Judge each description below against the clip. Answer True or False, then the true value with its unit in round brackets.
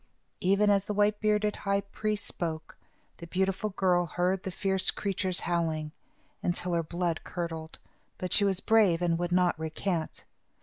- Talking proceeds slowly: False (160 wpm)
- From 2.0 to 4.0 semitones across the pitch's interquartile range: True (2.7 semitones)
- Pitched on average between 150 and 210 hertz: True (185 Hz)